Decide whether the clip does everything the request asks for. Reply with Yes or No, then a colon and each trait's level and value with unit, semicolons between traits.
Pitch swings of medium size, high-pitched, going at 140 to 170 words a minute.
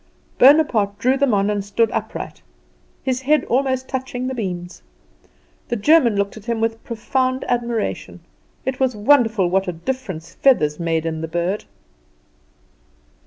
Yes: average, 5.0 semitones; high, 225 Hz; average, 145 wpm